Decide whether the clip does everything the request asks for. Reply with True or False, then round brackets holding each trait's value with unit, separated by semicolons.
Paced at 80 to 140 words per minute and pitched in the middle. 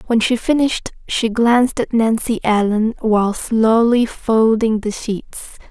False (135 wpm; 225 Hz)